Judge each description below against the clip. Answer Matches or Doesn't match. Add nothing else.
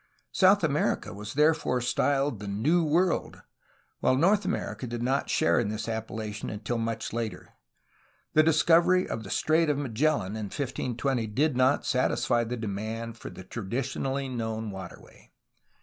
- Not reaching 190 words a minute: Matches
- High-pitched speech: Doesn't match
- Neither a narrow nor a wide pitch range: Matches